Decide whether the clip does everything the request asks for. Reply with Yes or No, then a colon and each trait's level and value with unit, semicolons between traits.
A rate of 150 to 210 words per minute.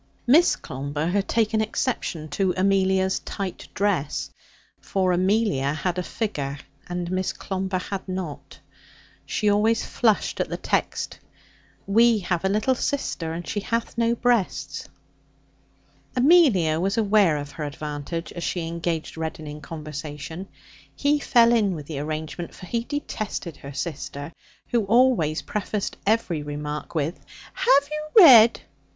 No: average, 140 wpm